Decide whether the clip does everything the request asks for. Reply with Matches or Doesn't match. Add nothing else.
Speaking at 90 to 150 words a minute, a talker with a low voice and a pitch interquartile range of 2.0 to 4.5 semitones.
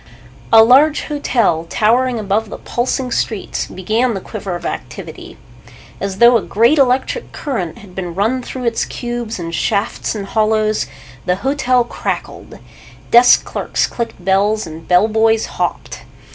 Doesn't match